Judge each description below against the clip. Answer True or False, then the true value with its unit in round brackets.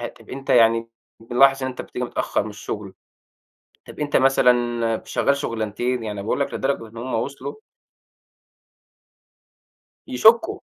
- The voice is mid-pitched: False (120 Hz)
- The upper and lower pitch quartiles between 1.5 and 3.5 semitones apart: True (3.0 semitones)